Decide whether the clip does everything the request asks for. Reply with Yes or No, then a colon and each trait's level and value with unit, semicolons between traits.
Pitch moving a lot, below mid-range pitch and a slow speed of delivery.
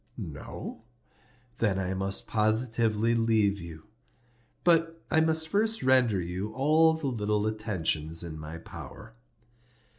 Yes: wide, 5.9 semitones; low, 110 Hz; slow, 120 wpm